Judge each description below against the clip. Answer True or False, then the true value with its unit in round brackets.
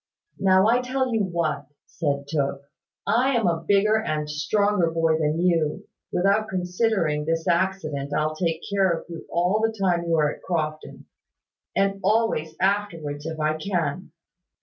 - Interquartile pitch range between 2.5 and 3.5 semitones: False (4.5 semitones)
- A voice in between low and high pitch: True (170 Hz)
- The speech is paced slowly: False (155 wpm)